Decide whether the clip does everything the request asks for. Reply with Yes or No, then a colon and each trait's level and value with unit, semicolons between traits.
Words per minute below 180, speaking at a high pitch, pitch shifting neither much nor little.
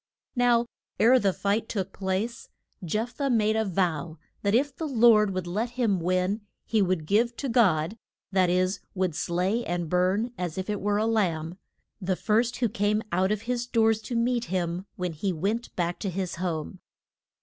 No: average, 185 wpm; high, 200 Hz; average, 4.0 semitones